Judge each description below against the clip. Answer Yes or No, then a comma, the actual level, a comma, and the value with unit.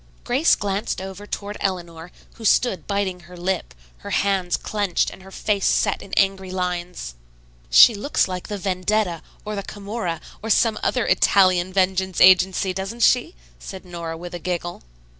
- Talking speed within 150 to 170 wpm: Yes, average, 160 wpm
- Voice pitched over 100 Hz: Yes, high, 190 Hz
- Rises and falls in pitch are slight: Yes, narrow, 2.3 semitones